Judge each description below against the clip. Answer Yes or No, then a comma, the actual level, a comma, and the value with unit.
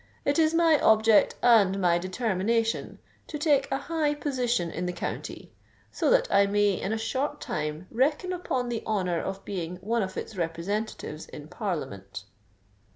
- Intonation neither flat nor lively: No, wide, 7.0 semitones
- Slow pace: No, average, 155 wpm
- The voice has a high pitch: Yes, high, 215 Hz